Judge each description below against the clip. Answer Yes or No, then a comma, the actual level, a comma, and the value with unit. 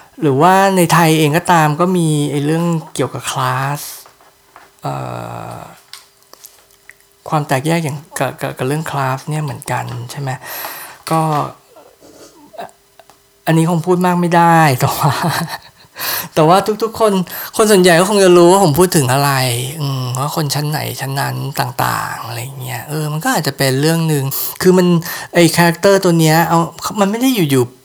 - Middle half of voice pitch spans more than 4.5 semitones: No, average, 4.2 semitones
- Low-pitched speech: No, medium, 155 Hz